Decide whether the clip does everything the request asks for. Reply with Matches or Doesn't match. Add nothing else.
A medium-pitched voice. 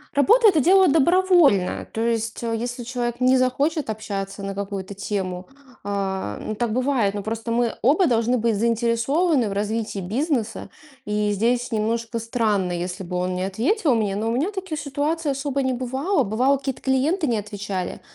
Doesn't match